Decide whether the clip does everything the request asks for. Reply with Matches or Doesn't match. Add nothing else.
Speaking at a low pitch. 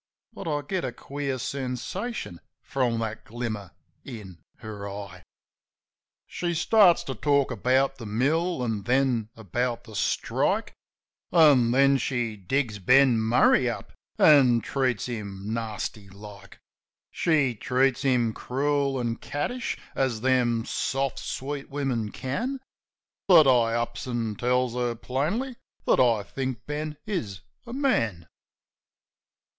Matches